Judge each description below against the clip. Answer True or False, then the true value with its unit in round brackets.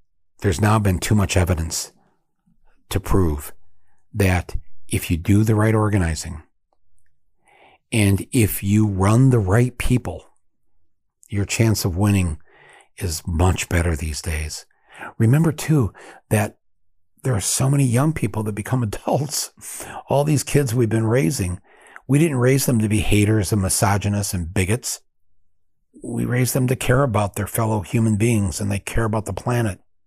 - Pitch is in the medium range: False (100 Hz)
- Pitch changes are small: False (4.4 semitones)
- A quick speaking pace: False (150 wpm)